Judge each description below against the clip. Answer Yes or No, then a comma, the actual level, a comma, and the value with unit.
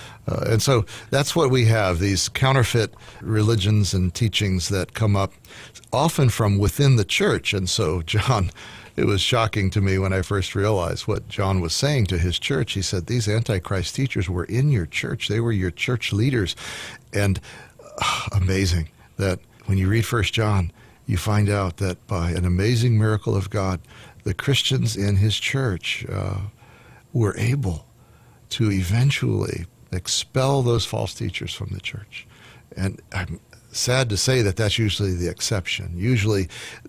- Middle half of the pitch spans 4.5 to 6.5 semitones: No, average, 3.7 semitones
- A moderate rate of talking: Yes, average, 165 wpm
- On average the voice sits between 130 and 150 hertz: No, low, 105 Hz